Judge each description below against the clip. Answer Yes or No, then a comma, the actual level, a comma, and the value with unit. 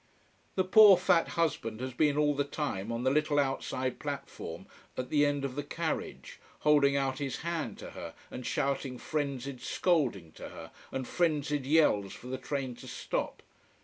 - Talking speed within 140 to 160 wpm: No, average, 175 wpm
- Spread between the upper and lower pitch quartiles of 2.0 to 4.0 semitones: Yes, average, 2.8 semitones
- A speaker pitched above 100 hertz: Yes, medium, 140 Hz